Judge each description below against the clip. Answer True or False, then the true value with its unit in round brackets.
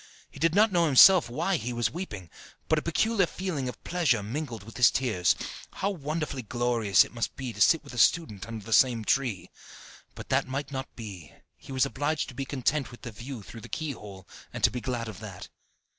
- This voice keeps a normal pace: False (215 wpm)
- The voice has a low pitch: True (130 Hz)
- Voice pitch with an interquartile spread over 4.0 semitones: True (5.3 semitones)